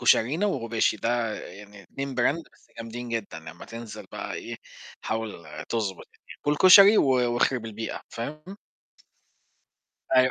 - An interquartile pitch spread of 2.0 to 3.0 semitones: No, average, 3.6 semitones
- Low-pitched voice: Yes, low, 115 Hz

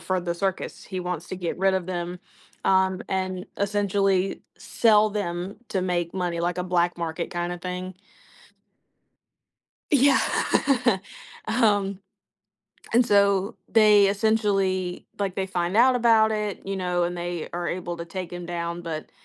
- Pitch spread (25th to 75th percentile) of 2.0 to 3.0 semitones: Yes, narrow, 2.4 semitones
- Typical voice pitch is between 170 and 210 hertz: Yes, medium, 185 Hz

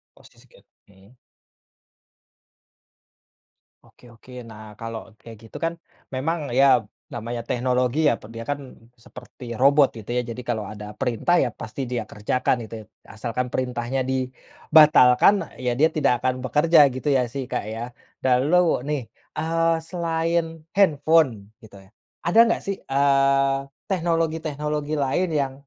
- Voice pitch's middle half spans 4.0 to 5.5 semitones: Yes, average, 4.6 semitones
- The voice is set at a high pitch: No, low, 135 Hz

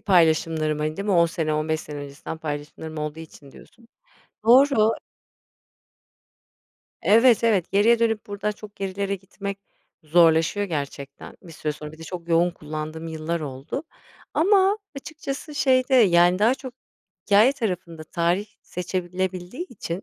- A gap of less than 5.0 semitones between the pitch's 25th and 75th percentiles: No, wide, 5.5 semitones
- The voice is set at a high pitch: No, medium, 180 Hz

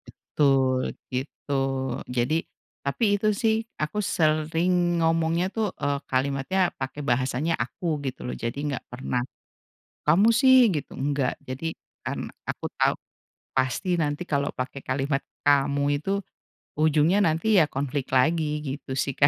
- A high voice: No, medium, 150 Hz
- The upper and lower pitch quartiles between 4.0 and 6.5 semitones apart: Yes, average, 4.3 semitones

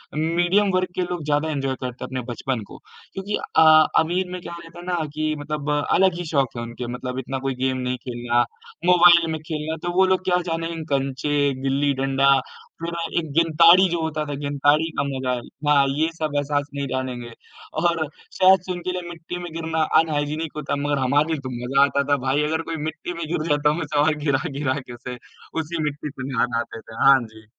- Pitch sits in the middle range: Yes, medium, 150 Hz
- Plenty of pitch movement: No, average, 3.6 semitones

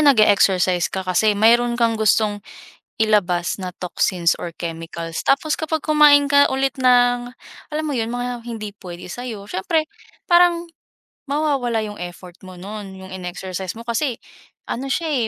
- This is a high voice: Yes, high, 225 Hz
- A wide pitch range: Yes, wide, 6.3 semitones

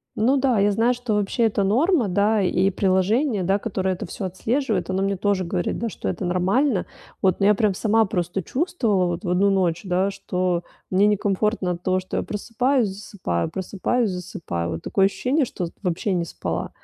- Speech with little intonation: No, average, 3.3 semitones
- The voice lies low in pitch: No, high, 195 Hz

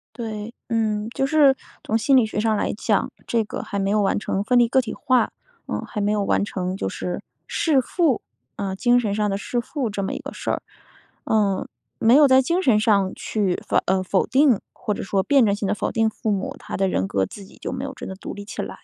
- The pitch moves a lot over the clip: No, average, 3.8 semitones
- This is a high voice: Yes, high, 215 Hz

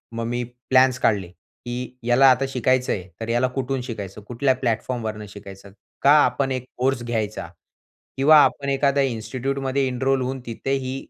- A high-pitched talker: No, low, 125 Hz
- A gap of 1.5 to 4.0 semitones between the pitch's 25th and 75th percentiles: Yes, narrow, 2.5 semitones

